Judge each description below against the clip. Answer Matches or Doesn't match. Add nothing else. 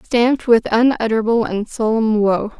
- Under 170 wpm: Matches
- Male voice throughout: Doesn't match